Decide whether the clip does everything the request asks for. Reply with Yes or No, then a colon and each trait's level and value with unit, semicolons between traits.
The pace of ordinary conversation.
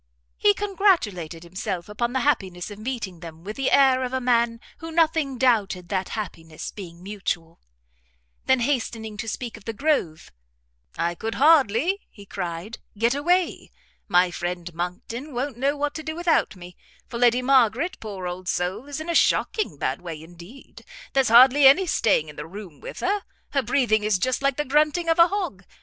Yes: average, 180 wpm